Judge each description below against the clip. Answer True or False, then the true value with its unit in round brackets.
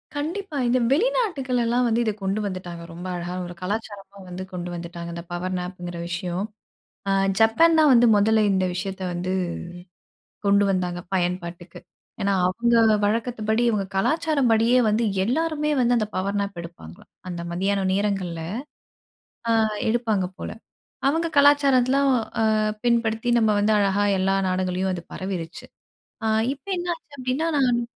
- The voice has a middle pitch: False (205 Hz)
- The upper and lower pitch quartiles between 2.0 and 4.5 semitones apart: False (5.0 semitones)